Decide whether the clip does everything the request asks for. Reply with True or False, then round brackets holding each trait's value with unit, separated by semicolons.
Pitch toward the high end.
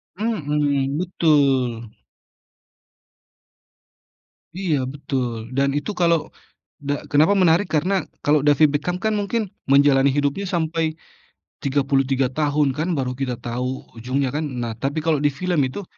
False (145 Hz)